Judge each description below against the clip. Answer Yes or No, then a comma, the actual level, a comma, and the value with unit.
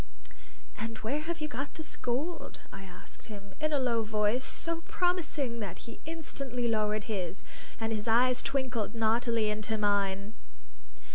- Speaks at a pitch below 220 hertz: No, high, 230 Hz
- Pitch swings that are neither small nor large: Yes, average, 4.4 semitones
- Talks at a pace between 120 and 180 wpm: Yes, average, 150 wpm